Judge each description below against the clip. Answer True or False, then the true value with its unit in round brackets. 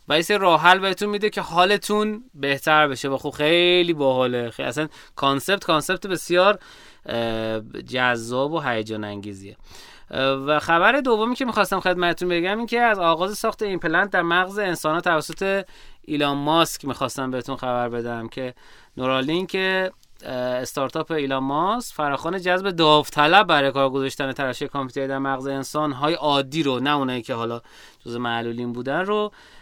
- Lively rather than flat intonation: True (5.7 semitones)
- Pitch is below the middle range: False (150 Hz)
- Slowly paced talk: False (155 wpm)